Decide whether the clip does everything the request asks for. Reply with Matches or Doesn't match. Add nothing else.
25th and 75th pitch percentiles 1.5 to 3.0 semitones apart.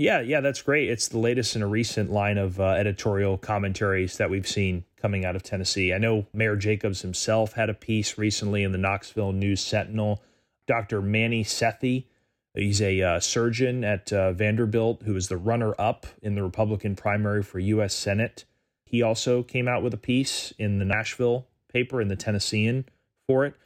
Matches